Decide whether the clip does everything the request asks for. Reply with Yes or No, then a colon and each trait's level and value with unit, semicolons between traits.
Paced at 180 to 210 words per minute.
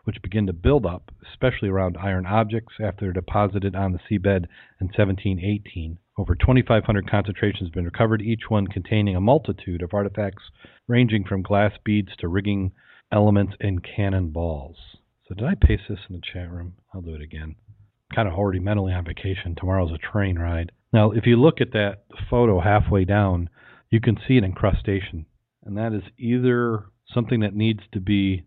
Yes: average, 190 wpm